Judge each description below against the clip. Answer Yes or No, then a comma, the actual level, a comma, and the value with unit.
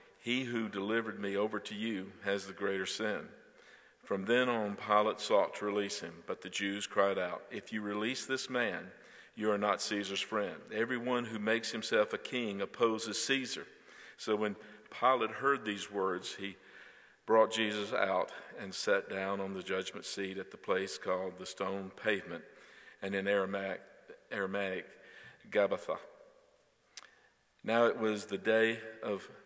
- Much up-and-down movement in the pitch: No, narrow, 2.6 semitones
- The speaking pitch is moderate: No, low, 105 Hz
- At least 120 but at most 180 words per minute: Yes, average, 155 wpm